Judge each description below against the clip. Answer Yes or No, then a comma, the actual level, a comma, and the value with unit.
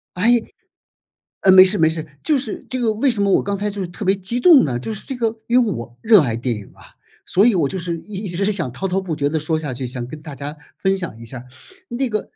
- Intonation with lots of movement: Yes, wide, 6.4 semitones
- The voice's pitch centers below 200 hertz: Yes, high, 190 Hz